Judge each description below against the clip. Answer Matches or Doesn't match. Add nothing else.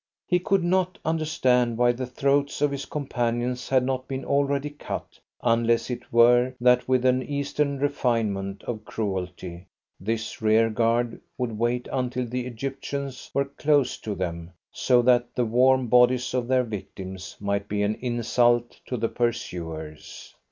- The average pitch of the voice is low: Matches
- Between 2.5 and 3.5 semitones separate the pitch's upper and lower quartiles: Matches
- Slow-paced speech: Doesn't match